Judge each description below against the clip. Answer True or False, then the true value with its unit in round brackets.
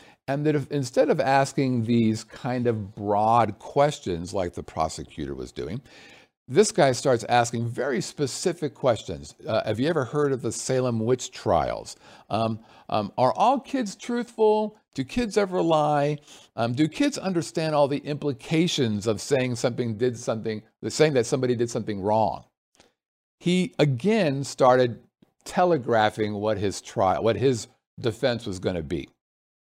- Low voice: True (130 Hz)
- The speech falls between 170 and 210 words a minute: False (155 wpm)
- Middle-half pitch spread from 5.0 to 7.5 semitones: True (5.3 semitones)